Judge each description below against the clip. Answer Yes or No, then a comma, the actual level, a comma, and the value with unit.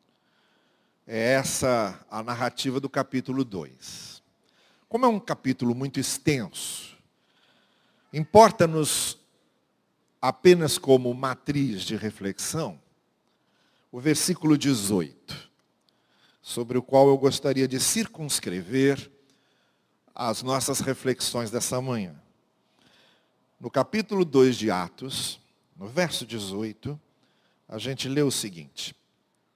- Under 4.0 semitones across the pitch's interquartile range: Yes, average, 3.1 semitones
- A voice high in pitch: No, low, 130 Hz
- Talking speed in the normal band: No, slow, 95 wpm